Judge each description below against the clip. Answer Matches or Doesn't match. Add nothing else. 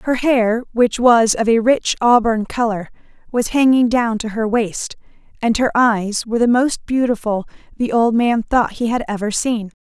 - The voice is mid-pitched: Doesn't match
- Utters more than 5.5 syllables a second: Doesn't match